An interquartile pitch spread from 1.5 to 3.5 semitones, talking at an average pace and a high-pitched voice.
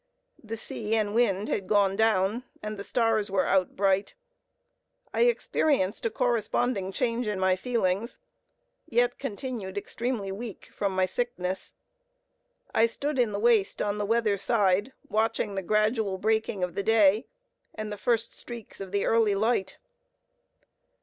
Yes: average, 2.9 semitones; average, 150 wpm; high, 215 Hz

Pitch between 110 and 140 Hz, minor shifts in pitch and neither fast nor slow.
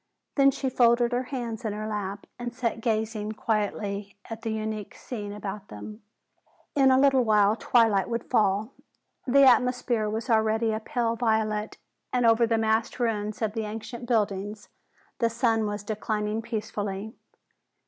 No: high, 220 Hz; narrow, 2.1 semitones; average, 155 wpm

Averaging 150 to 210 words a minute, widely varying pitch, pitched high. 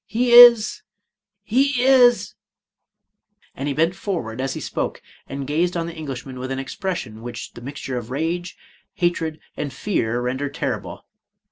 No: average, 165 wpm; wide, 7.5 semitones; medium, 160 Hz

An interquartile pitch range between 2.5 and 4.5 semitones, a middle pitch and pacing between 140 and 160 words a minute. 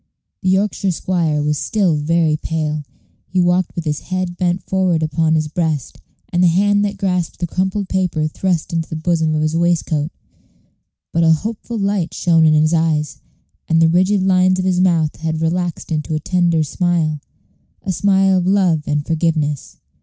No: average, 2.9 semitones; medium, 170 Hz; average, 175 wpm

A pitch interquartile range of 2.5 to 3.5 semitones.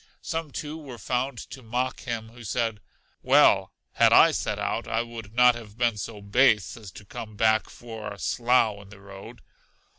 Yes: average, 2.9 semitones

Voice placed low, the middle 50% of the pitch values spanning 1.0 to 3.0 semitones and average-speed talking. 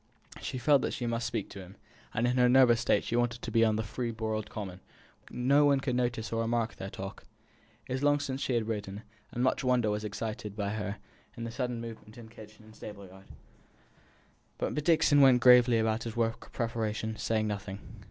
No: low, 115 Hz; narrow, 2.4 semitones; fast, 210 wpm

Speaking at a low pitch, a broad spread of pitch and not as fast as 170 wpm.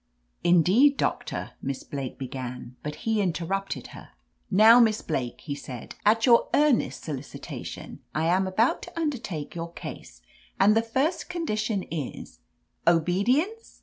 No: high, 190 Hz; wide, 7.4 semitones; average, 150 wpm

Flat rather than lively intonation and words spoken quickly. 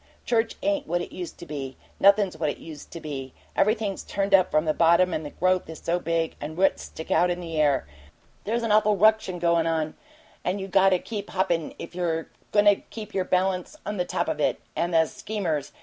No: average, 3.6 semitones; fast, 225 wpm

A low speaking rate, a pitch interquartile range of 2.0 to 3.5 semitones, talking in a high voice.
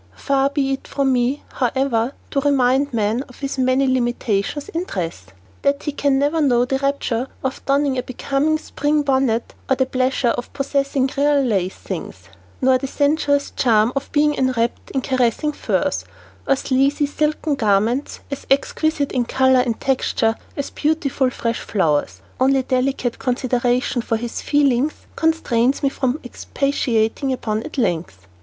No: average, 155 wpm; average, 2.7 semitones; very high, 265 Hz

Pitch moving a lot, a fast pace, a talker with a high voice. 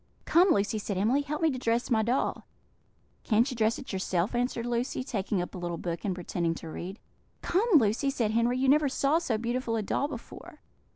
No: average, 4.8 semitones; fast, 210 wpm; high, 235 Hz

